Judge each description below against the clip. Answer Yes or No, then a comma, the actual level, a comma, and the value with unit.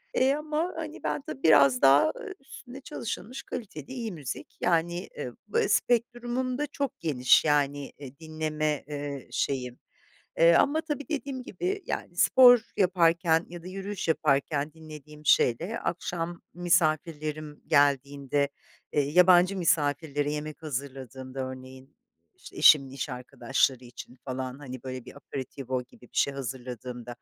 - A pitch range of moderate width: No, wide, 6.0 semitones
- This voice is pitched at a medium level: Yes, medium, 155 Hz